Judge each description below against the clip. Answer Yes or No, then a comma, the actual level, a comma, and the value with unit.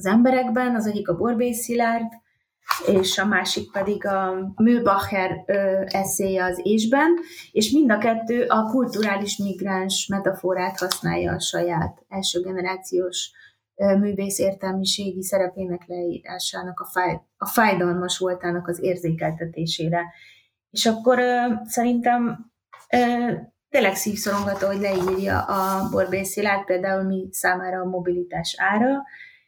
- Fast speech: No, average, 115 wpm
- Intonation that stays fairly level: No, average, 3.7 semitones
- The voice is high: Yes, high, 195 Hz